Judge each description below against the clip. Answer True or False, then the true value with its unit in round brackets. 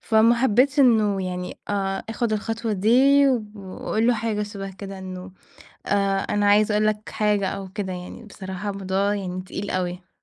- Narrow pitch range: True (2.3 semitones)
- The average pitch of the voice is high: True (205 Hz)